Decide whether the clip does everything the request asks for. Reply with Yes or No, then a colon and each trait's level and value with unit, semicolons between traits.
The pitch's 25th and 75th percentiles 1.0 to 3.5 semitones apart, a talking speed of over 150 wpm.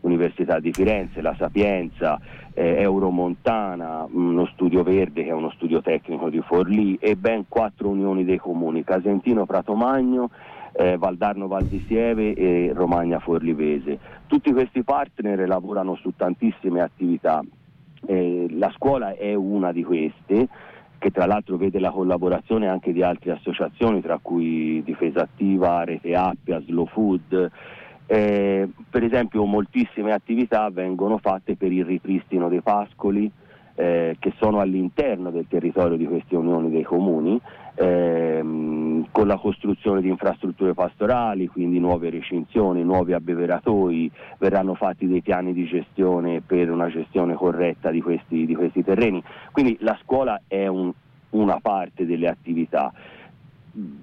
No: average, 2.8 semitones; average, 135 wpm